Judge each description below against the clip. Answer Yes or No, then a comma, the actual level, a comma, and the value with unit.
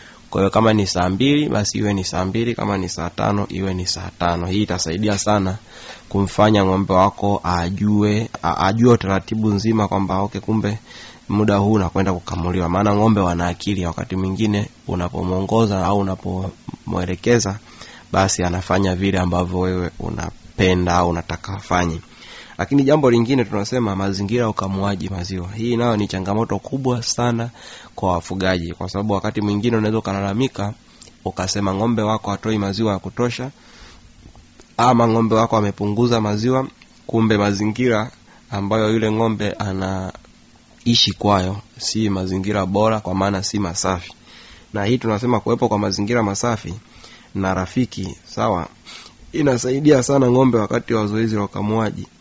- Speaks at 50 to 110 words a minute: No, average, 135 wpm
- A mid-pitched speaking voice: No, low, 100 Hz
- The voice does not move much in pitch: No, average, 3.0 semitones